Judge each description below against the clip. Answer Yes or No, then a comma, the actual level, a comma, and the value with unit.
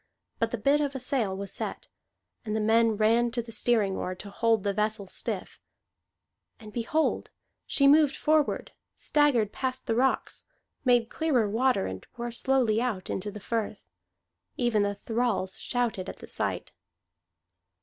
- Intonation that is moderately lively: Yes, average, 3.3 semitones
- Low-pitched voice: No, high, 230 Hz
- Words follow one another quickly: No, average, 155 wpm